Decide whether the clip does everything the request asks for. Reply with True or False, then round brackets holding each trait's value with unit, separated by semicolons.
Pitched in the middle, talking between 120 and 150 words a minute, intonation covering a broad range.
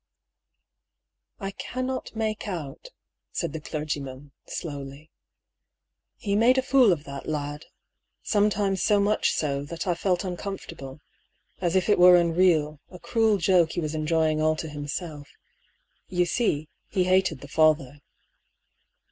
False (170 Hz; 140 wpm; 4.7 semitones)